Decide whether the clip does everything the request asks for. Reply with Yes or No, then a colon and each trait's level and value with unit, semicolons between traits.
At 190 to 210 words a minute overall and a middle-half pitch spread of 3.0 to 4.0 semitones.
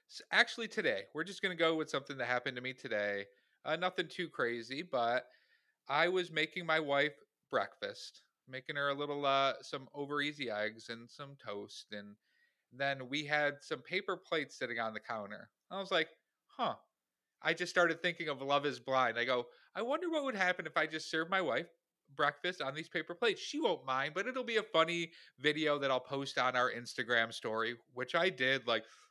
No: average, 200 wpm; average, 5.3 semitones